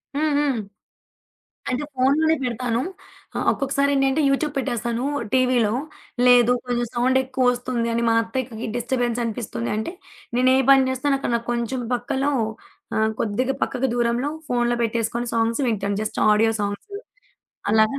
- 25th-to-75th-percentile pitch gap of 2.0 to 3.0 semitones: Yes, narrow, 2.4 semitones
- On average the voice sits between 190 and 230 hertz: No, high, 245 Hz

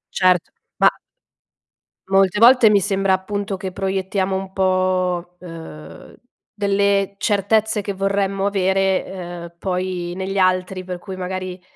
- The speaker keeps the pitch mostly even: Yes, narrow, 1.3 semitones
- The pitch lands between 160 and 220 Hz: Yes, high, 190 Hz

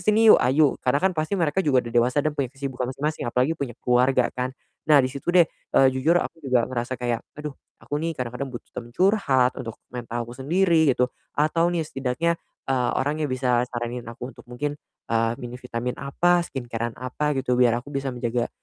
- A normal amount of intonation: Yes, average, 3.6 semitones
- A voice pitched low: Yes, low, 130 Hz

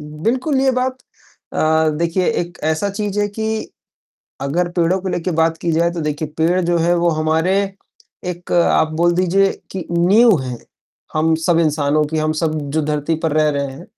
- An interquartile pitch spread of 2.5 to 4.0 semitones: Yes, average, 3.1 semitones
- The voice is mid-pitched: Yes, medium, 170 Hz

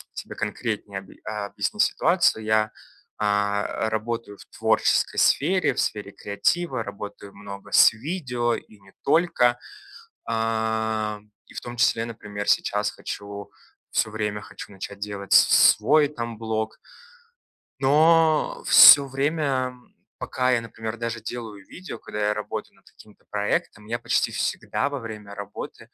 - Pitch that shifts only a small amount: No, average, 3.6 semitones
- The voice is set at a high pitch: No, low, 110 Hz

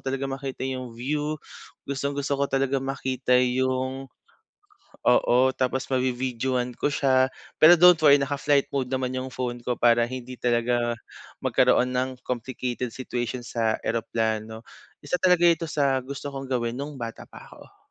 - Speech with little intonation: Yes, narrow, 1.9 semitones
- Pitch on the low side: Yes, low, 130 Hz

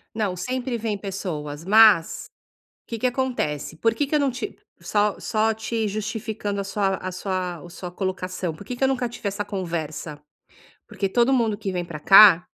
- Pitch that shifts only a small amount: No, average, 3.7 semitones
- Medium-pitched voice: No, high, 205 Hz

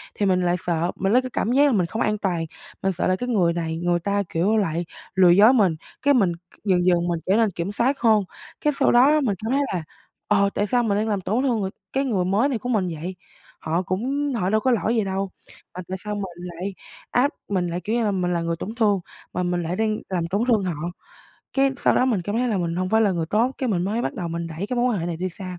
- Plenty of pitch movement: No, average, 4.3 semitones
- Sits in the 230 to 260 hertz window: No, high, 195 Hz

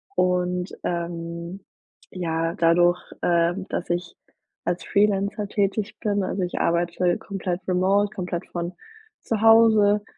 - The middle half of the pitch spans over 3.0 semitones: No, average, 2.7 semitones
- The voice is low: No, medium, 180 Hz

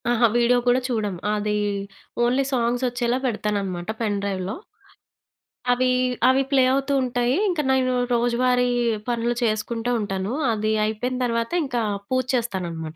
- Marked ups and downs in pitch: No, average, 2.8 semitones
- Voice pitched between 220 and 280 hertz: Yes, high, 235 Hz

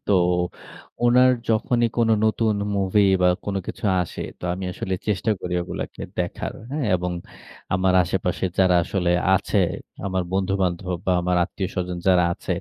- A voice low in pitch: Yes, very low, 95 Hz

